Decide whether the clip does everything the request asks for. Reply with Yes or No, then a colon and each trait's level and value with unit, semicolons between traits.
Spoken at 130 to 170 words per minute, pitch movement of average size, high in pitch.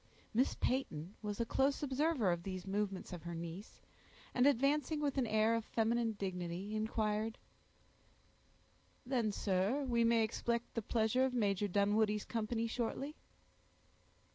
Yes: average, 140 wpm; average, 3.6 semitones; high, 220 Hz